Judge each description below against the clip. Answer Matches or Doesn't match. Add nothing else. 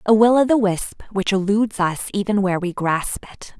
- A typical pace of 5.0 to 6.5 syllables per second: Matches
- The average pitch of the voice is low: Doesn't match